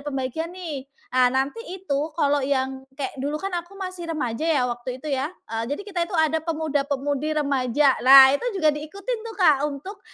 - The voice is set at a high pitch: Yes, very high, 290 Hz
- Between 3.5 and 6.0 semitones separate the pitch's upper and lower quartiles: Yes, average, 3.9 semitones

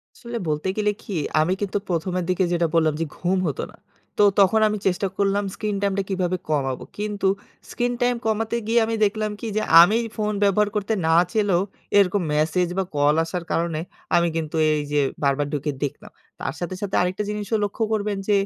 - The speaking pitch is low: No, high, 195 Hz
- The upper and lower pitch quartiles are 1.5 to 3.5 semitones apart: No, average, 4.1 semitones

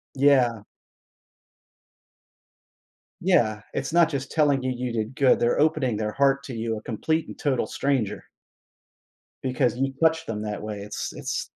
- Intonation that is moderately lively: Yes, average, 4.1 semitones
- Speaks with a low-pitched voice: Yes, low, 130 Hz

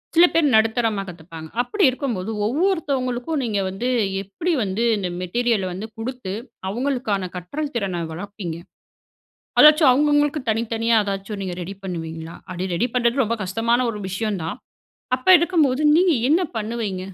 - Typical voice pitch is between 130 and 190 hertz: No, high, 225 Hz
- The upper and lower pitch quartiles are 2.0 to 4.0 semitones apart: No, wide, 5.4 semitones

